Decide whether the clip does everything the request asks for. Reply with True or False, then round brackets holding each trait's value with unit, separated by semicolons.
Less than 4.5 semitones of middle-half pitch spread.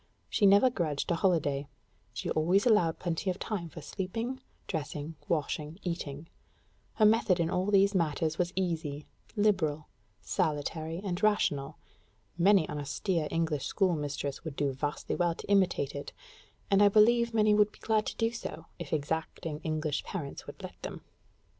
False (4.9 semitones)